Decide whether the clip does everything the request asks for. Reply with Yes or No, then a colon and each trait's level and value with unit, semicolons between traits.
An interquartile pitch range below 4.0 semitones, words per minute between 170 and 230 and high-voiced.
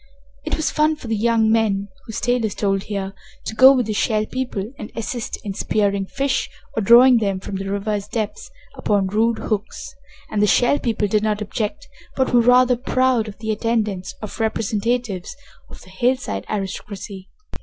Yes: average, 3.2 semitones; average, 180 wpm; high, 220 Hz